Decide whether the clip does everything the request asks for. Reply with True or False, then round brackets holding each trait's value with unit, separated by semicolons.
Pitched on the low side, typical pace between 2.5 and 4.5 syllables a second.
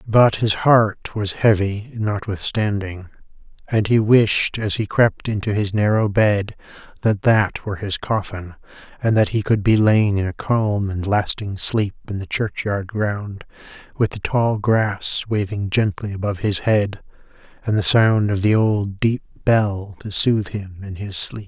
True (105 Hz; 4.1 syllables/s)